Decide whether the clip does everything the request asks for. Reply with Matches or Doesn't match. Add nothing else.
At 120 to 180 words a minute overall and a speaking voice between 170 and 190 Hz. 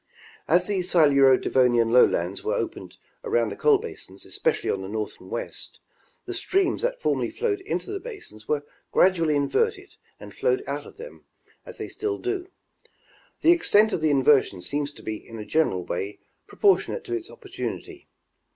Matches